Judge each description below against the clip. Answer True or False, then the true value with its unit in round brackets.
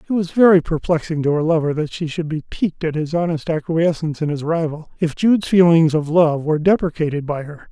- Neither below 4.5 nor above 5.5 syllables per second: False (5.9 syllables/s)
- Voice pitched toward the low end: False (160 Hz)